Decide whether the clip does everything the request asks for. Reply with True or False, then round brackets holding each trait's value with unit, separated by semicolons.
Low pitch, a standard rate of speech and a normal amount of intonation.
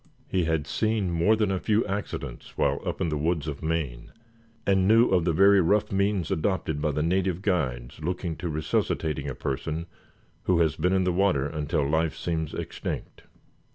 True (85 Hz; 185 wpm; 3.8 semitones)